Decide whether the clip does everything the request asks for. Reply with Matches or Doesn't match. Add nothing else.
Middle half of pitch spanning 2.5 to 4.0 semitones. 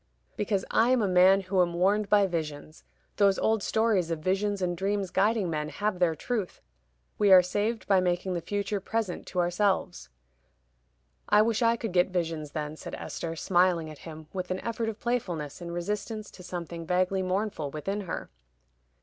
Matches